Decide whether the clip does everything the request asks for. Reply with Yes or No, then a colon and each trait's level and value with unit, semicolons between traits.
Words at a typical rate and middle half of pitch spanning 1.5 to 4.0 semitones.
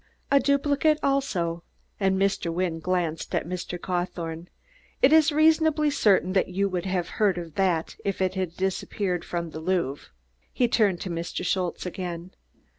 Yes: average, 160 wpm; average, 3.5 semitones